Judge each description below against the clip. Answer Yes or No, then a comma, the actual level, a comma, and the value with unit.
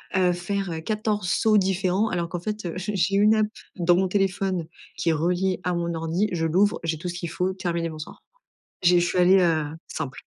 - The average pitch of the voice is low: No, medium, 180 Hz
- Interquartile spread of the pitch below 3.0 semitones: Yes, narrow, 2.4 semitones